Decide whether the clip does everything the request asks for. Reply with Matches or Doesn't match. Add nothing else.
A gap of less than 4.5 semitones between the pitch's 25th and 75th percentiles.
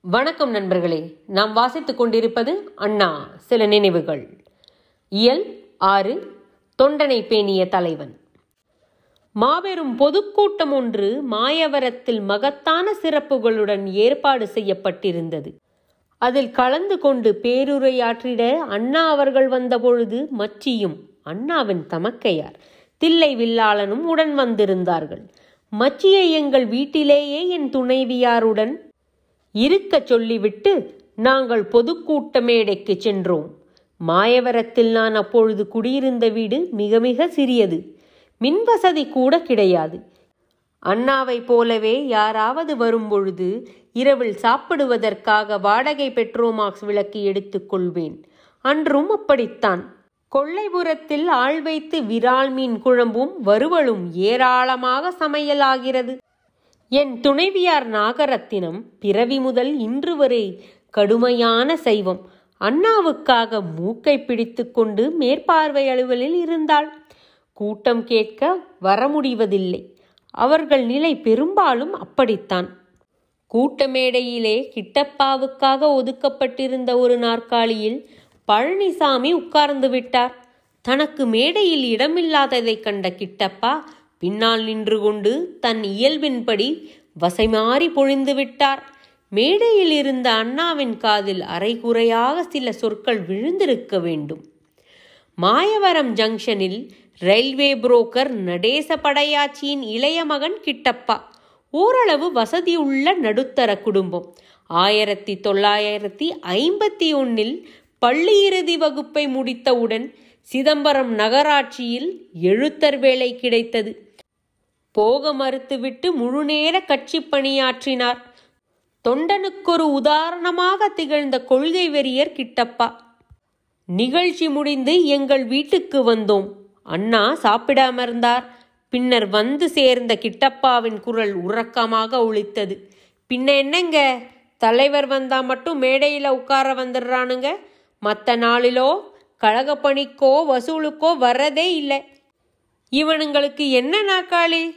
Doesn't match